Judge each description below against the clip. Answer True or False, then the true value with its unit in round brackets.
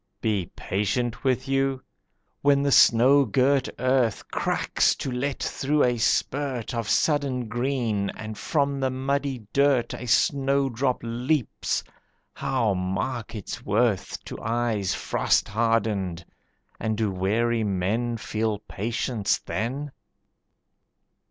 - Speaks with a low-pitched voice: True (120 Hz)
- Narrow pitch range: False (3.9 semitones)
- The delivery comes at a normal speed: False (115 wpm)